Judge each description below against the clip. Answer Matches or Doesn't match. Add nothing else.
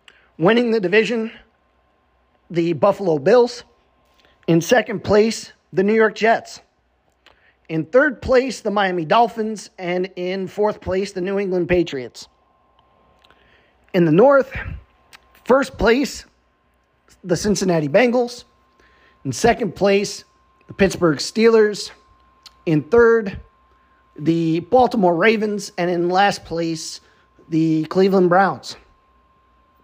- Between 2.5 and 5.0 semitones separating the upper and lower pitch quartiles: Doesn't match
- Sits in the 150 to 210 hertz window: Matches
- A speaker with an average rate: Doesn't match